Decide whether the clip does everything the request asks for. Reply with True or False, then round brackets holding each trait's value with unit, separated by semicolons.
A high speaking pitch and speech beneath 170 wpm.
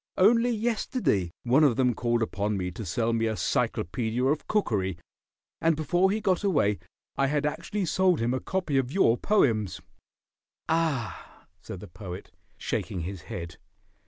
False (130 Hz; 160 wpm)